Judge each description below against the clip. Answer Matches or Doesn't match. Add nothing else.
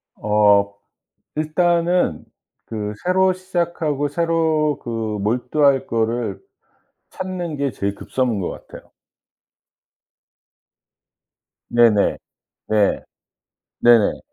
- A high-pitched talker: Doesn't match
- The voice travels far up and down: Matches